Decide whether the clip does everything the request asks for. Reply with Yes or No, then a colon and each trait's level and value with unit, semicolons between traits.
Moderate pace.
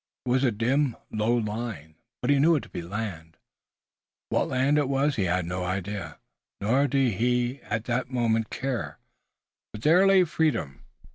Yes: average, 170 wpm